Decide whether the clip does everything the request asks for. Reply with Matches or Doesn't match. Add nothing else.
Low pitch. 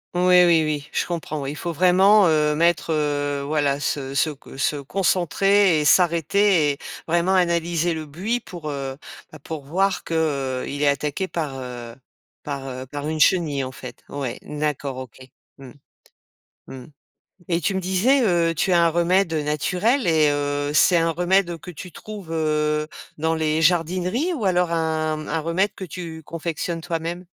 Doesn't match